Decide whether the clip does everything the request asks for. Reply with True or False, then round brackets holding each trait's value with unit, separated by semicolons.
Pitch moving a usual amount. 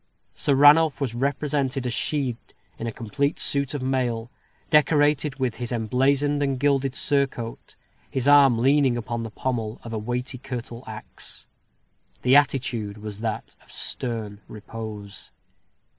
True (3.5 semitones)